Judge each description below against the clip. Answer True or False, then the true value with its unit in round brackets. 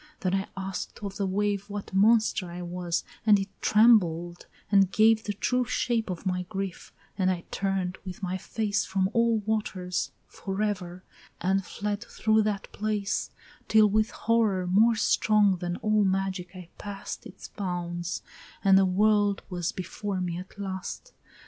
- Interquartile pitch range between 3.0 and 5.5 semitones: False (2.6 semitones)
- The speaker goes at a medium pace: True (155 wpm)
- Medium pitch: False (195 Hz)